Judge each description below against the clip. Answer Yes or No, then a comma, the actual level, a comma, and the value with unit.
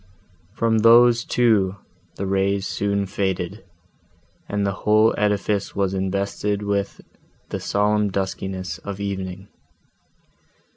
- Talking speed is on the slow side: Yes, slow, 105 wpm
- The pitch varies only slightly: Yes, narrow, 1.5 semitones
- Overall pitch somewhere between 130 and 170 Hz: No, low, 100 Hz